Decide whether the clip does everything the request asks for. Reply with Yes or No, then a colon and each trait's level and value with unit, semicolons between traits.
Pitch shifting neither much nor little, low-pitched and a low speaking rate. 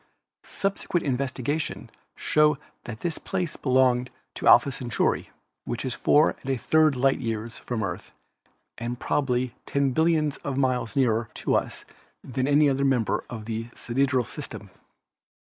No: average, 3.1 semitones; low, 130 Hz; average, 150 wpm